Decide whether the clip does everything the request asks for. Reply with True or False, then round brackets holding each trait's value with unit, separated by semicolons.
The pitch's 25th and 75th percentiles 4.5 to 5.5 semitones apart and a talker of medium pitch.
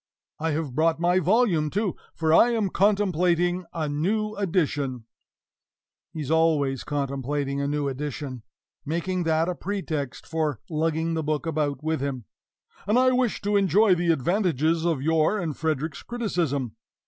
False (3.9 semitones; 160 Hz)